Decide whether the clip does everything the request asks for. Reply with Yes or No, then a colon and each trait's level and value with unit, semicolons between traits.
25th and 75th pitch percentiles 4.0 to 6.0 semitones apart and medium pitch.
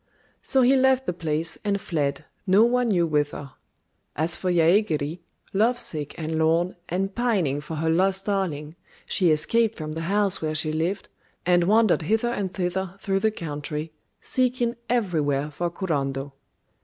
Yes: average, 4.9 semitones; medium, 175 Hz